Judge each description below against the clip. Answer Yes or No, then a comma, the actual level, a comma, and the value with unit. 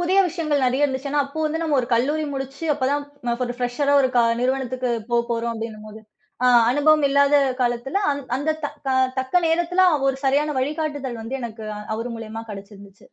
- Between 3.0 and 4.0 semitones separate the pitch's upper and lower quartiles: Yes, average, 3.7 semitones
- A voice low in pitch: No, very high, 265 Hz